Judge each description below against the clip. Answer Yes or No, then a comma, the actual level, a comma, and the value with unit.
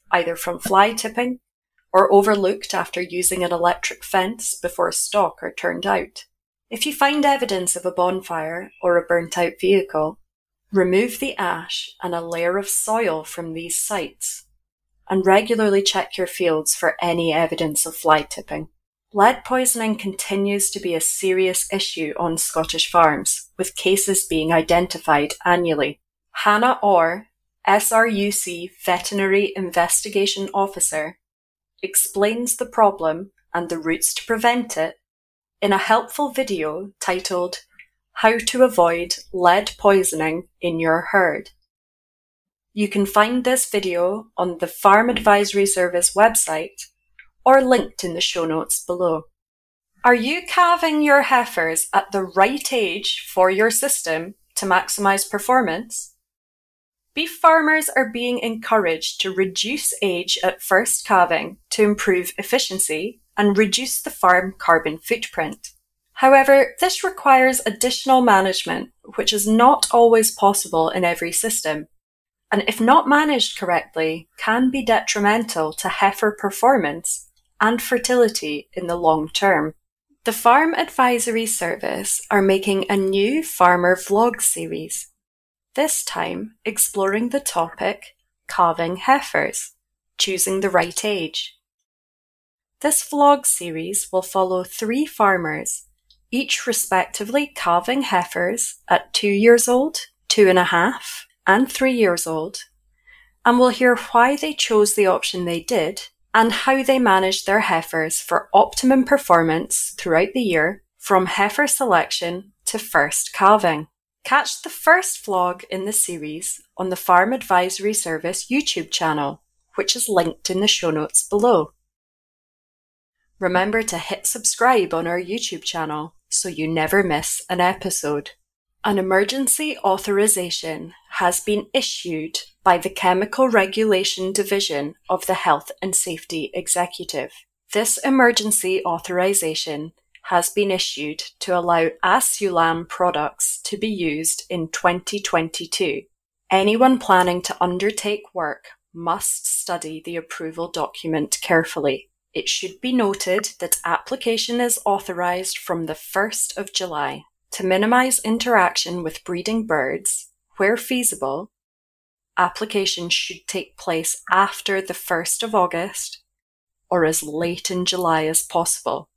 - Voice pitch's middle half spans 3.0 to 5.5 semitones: Yes, average, 4.7 semitones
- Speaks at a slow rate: Yes, slow, 130 wpm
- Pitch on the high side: Yes, high, 195 Hz